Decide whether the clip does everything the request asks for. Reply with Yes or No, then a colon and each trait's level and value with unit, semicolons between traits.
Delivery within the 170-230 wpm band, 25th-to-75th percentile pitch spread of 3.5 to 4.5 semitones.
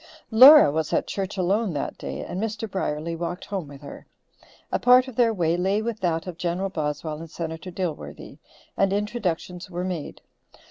Yes: average, 180 wpm; average, 4.1 semitones